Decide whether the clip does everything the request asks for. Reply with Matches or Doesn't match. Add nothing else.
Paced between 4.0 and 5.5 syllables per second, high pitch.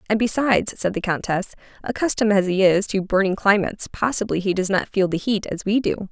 Doesn't match